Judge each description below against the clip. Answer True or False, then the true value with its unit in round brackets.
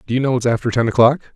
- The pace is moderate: False (310 wpm)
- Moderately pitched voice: False (125 Hz)